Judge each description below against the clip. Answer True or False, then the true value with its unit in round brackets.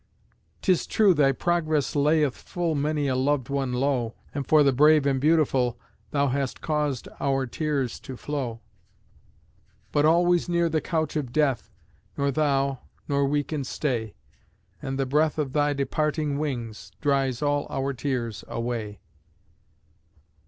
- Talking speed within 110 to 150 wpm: True (145 wpm)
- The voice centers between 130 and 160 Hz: True (140 Hz)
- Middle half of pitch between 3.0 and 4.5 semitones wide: False (2.5 semitones)